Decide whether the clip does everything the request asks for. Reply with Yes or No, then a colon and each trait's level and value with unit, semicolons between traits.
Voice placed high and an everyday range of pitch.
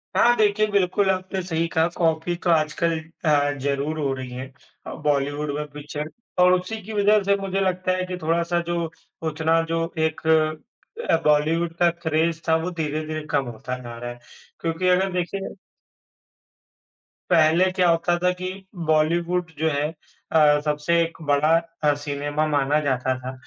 No: medium, 160 Hz; average, 3.3 semitones